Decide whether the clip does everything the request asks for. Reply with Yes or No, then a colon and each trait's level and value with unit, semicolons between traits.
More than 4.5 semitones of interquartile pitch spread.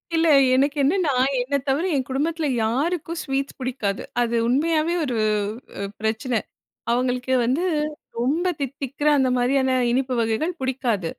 No: average, 3.6 semitones